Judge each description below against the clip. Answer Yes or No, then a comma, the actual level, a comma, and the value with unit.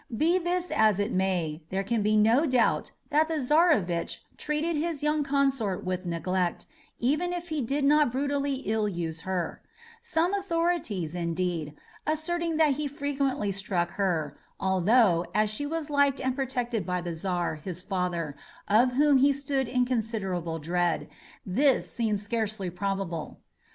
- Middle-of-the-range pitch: No, high, 225 Hz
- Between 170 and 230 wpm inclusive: No, average, 150 wpm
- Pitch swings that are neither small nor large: No, wide, 7.9 semitones